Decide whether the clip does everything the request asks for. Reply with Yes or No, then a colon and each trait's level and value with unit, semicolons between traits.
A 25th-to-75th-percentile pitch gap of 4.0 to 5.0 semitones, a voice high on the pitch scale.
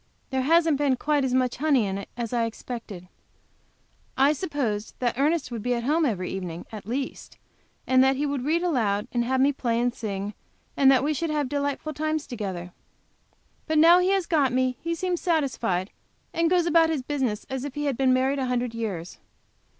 Yes: average, 4.5 semitones; very high, 265 Hz